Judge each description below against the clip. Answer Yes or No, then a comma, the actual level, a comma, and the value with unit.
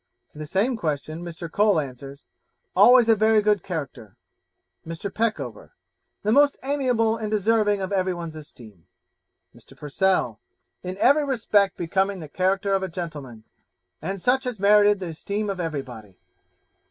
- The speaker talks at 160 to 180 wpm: No, average, 150 wpm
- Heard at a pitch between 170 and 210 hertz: Yes, high, 190 Hz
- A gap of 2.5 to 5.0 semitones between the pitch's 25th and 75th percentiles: No, wide, 5.4 semitones